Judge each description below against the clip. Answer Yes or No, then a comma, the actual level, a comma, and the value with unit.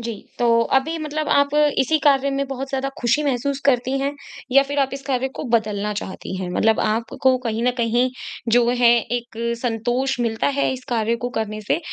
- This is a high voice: Yes, high, 245 Hz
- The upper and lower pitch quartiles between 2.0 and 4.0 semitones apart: Yes, average, 3.0 semitones